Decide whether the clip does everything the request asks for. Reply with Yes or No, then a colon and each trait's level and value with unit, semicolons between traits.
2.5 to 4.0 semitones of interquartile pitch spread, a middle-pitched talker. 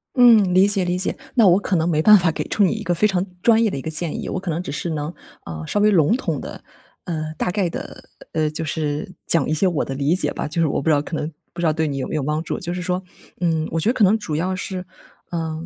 Yes: average, 3.5 semitones; medium, 170 Hz